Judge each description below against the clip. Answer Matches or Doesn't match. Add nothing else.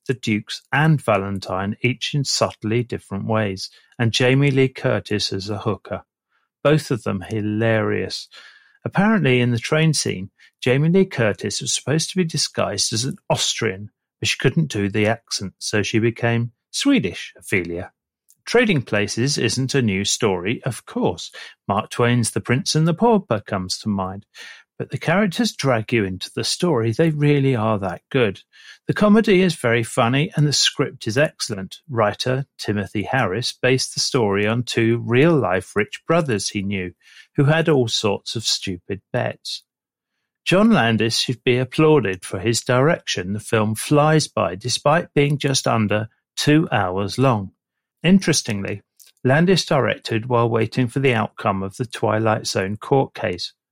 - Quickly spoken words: Doesn't match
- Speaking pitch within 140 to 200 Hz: Doesn't match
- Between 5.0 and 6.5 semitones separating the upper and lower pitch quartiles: Matches